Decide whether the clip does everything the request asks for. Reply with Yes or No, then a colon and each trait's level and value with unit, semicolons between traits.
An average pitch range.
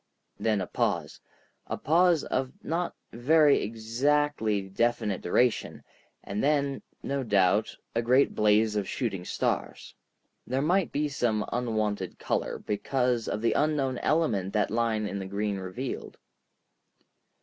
Yes: average, 5.0 semitones